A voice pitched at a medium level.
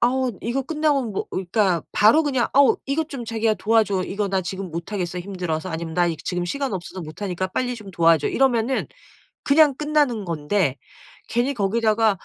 No: high, 210 Hz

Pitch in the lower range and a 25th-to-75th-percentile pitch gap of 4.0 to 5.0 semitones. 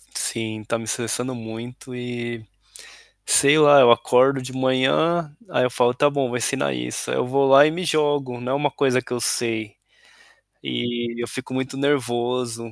No: low, 125 Hz; narrow, 2.5 semitones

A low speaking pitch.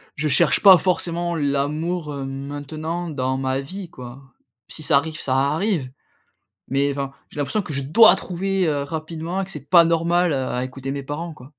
No: medium, 150 Hz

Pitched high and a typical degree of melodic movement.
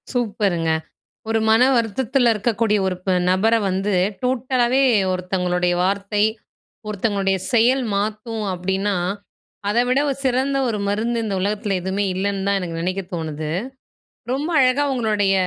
Yes: high, 210 Hz; average, 3.7 semitones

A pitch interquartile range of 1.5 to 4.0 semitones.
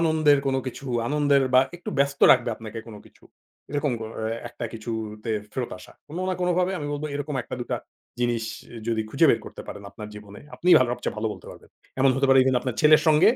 No: average, 4.7 semitones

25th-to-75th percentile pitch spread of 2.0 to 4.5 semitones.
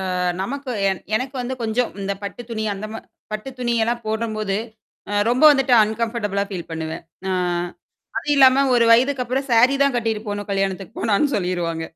Yes: average, 3.9 semitones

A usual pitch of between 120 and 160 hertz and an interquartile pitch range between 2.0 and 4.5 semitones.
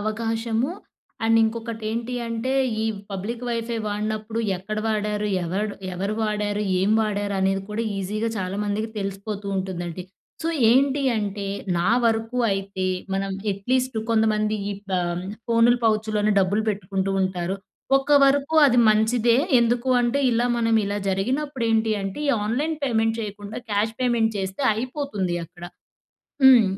No: high, 215 Hz; average, 2.8 semitones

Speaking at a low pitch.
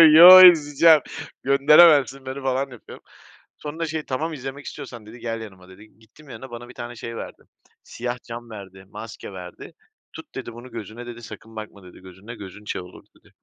Yes: low, 120 Hz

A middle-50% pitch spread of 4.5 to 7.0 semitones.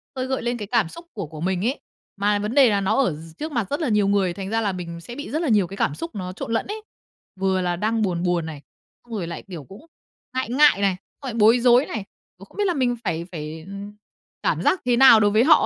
Yes: average, 5.2 semitones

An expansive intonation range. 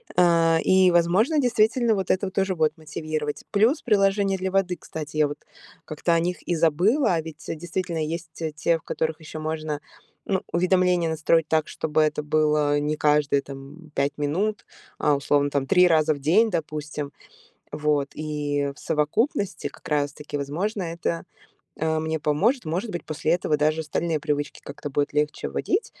No: average, 3.4 semitones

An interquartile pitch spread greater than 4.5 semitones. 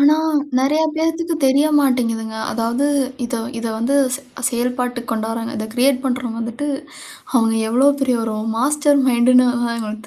No: average, 3.3 semitones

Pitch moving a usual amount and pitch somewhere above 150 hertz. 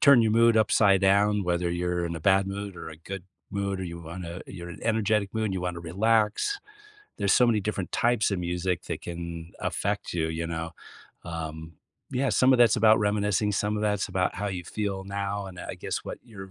No: average, 3.4 semitones; very low, 95 Hz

